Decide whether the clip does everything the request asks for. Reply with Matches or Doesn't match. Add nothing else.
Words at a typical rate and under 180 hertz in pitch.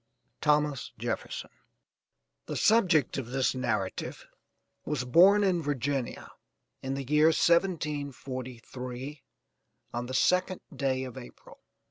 Doesn't match